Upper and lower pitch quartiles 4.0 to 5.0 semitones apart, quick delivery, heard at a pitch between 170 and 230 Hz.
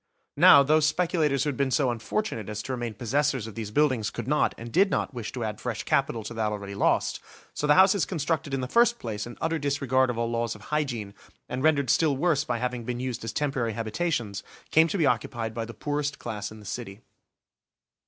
No: average, 4.7 semitones; fast, 220 wpm; low, 125 Hz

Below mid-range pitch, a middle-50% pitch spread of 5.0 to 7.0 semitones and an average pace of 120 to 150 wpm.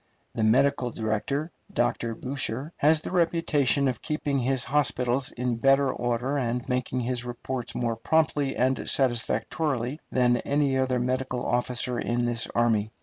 No: low, 125 Hz; narrow, 2.6 semitones; average, 145 wpm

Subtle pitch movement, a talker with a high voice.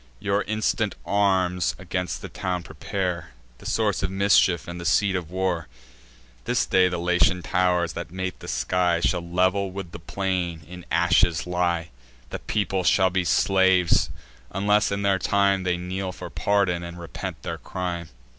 No: narrow, 1.7 semitones; very low, 90 Hz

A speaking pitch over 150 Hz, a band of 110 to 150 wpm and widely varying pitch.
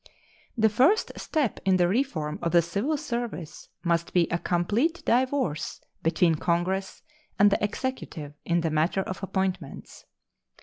Yes: high, 190 Hz; average, 140 wpm; wide, 5.8 semitones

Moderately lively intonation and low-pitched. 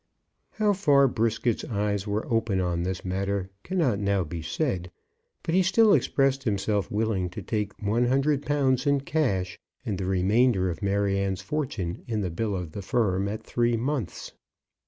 No: wide, 5.7 semitones; low, 105 Hz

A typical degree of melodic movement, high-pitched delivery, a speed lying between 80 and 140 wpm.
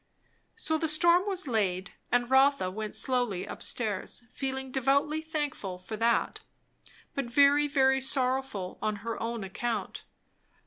Yes: average, 4.6 semitones; very high, 260 Hz; slow, 135 wpm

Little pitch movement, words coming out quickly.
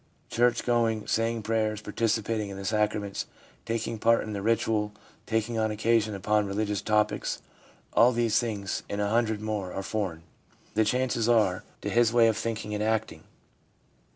No: narrow, 1.6 semitones; average, 160 wpm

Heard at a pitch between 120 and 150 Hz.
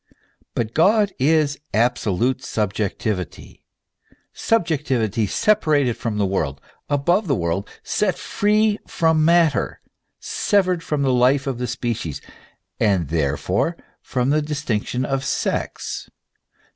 Yes: low, 135 Hz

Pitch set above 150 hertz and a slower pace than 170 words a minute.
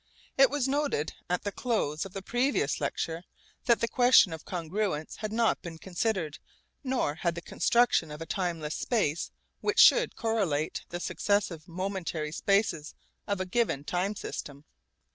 Yes: medium, 185 Hz; average, 155 wpm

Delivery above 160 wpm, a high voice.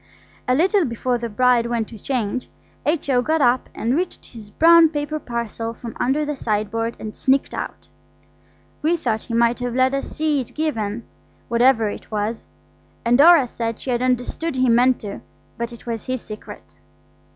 Yes: average, 175 wpm; high, 245 Hz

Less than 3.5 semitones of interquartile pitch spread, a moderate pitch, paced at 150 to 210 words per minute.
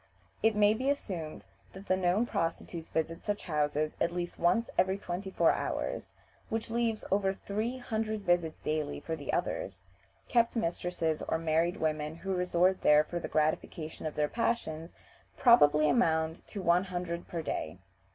No: average, 4.4 semitones; medium, 175 Hz; average, 160 wpm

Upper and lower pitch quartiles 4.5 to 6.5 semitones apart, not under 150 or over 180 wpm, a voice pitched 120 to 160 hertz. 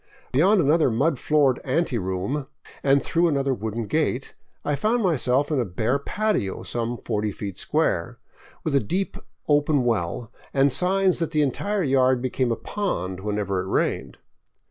Yes: wide, 5.6 semitones; average, 155 wpm; low, 135 Hz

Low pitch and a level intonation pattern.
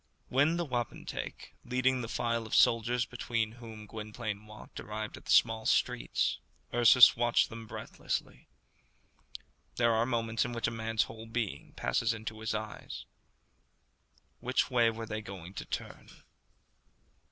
Yes: low, 115 Hz; narrow, 1.7 semitones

